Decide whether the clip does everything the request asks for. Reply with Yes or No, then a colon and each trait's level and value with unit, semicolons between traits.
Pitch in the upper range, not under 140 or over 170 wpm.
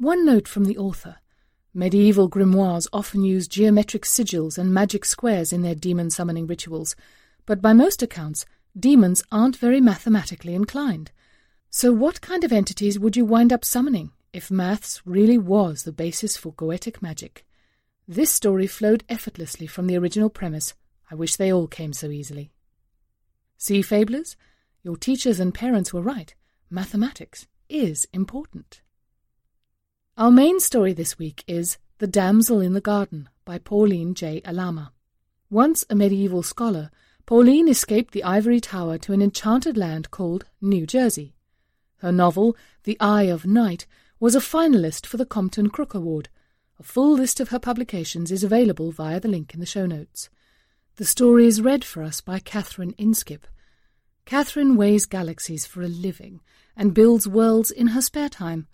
Yes: high, 200 Hz; average, 160 wpm